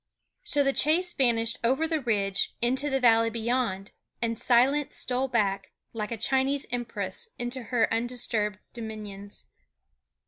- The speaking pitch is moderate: No, high, 240 Hz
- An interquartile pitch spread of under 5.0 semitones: Yes, average, 3.3 semitones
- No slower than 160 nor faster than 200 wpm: No, slow, 135 wpm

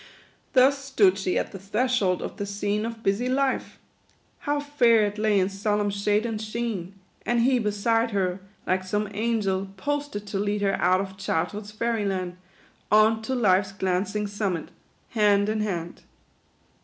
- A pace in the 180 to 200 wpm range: No, average, 165 wpm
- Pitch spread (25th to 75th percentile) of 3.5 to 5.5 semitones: No, average, 2.8 semitones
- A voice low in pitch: No, high, 210 Hz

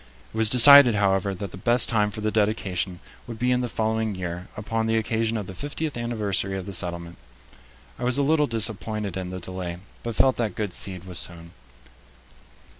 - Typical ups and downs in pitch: Yes, average, 3.9 semitones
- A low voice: Yes, low, 105 Hz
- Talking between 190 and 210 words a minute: Yes, average, 195 wpm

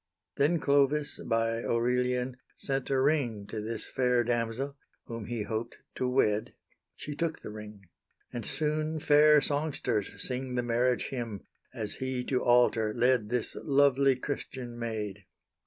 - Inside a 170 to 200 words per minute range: No, average, 140 wpm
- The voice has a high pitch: No, low, 125 Hz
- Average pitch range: Yes, average, 3.4 semitones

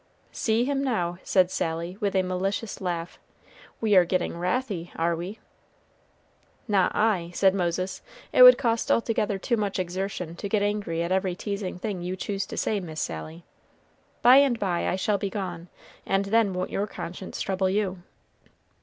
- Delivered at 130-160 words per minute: No, average, 170 wpm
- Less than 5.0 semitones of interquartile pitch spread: Yes, average, 2.9 semitones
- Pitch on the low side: No, high, 190 Hz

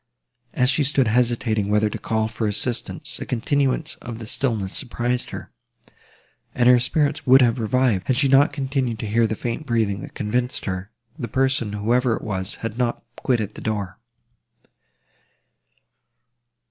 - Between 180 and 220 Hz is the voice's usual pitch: No, low, 120 Hz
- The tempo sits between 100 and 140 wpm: No, average, 160 wpm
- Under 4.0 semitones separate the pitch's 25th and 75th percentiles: Yes, average, 2.9 semitones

